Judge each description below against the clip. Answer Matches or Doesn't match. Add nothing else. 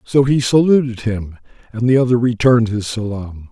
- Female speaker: Doesn't match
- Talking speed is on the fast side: Doesn't match